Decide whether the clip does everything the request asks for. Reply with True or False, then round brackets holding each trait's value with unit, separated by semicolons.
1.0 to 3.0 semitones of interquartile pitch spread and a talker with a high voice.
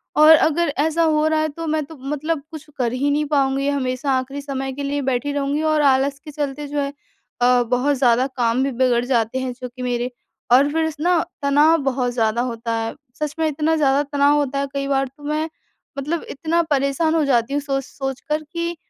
True (2.7 semitones; 280 Hz)